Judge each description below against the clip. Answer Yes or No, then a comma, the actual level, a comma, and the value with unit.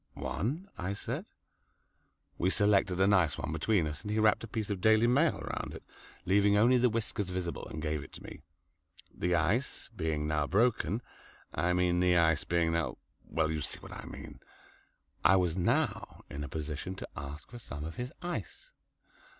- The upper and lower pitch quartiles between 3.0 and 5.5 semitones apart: Yes, average, 5.2 semitones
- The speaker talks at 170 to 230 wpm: Yes, average, 185 wpm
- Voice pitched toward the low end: Yes, very low, 90 Hz